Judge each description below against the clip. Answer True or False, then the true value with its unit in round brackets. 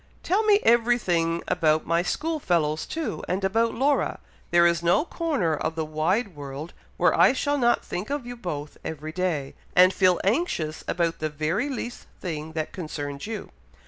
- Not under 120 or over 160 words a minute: False (175 wpm)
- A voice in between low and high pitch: True (180 Hz)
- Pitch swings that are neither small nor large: False (7.3 semitones)